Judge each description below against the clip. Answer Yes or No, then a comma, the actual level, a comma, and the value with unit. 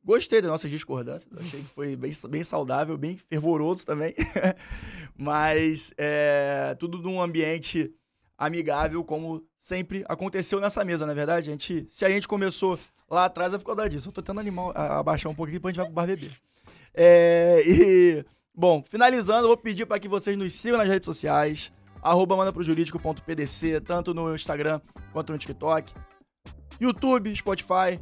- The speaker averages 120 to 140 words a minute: No, average, 165 wpm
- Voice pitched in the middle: Yes, medium, 170 Hz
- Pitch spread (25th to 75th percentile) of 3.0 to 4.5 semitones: Yes, average, 3.7 semitones